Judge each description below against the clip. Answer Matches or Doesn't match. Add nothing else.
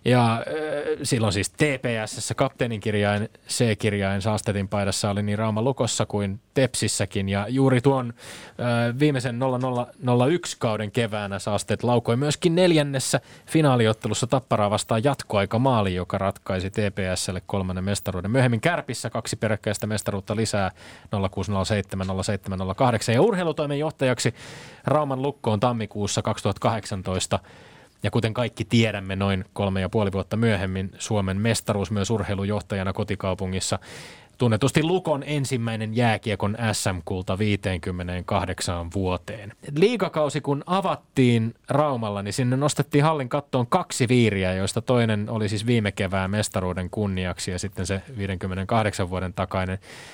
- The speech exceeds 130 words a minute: Doesn't match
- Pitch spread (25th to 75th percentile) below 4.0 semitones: Doesn't match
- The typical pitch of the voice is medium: Doesn't match